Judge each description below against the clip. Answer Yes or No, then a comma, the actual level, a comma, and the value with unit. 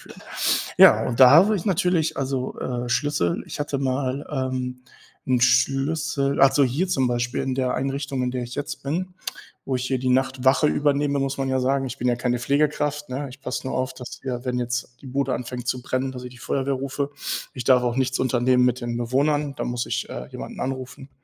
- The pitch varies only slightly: Yes, narrow, 1.8 semitones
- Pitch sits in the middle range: No, low, 130 Hz